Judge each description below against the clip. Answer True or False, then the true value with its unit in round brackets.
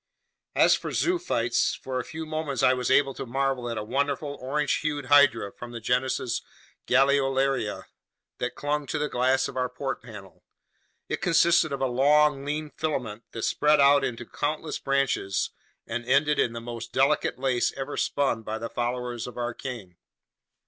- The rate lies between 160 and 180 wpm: True (170 wpm)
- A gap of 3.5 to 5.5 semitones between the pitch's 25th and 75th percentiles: False (3.1 semitones)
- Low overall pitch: True (130 Hz)